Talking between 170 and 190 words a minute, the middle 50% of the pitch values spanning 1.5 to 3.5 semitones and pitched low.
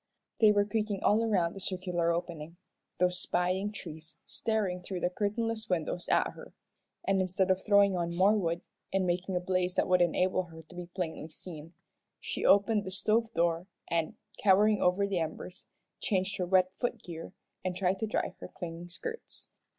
No: average, 180 wpm; narrow, 2.6 semitones; medium, 185 Hz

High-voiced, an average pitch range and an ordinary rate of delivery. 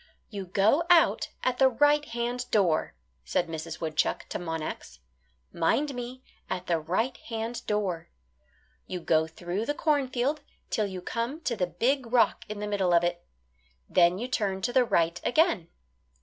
No: high, 210 Hz; wide, 6.3 semitones; average, 165 wpm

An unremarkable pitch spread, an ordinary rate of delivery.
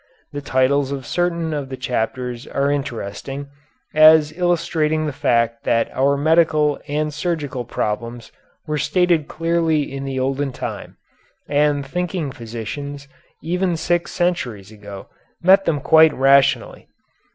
No: average, 3.5 semitones; slow, 130 wpm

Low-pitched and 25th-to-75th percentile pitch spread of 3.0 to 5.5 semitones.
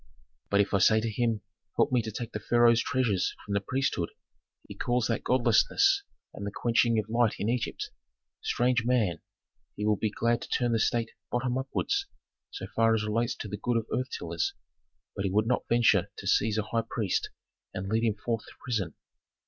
No: low, 115 Hz; narrow, 2.4 semitones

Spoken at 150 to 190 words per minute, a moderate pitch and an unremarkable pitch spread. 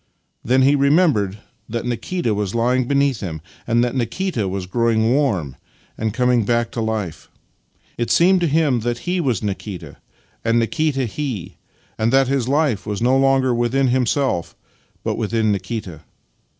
No: average, 160 wpm; low, 120 Hz; average, 3.8 semitones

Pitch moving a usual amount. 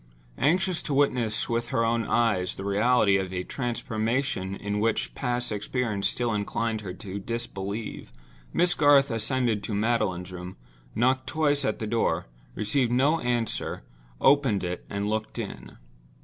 Yes: average, 3.8 semitones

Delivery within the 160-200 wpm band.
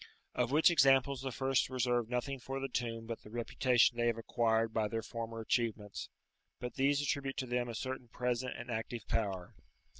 Yes: average, 185 wpm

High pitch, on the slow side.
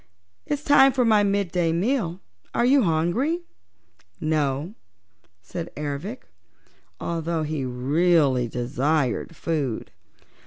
No: medium, 165 Hz; slow, 95 wpm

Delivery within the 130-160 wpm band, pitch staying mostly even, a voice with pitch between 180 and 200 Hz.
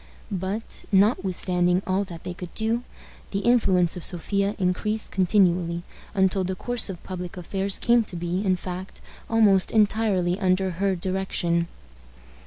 Yes: average, 140 wpm; narrow, 2.2 semitones; high, 190 Hz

